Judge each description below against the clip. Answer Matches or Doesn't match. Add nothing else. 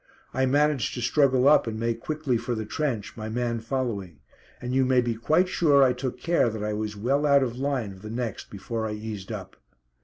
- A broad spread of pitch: Doesn't match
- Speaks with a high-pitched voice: Doesn't match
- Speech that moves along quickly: Matches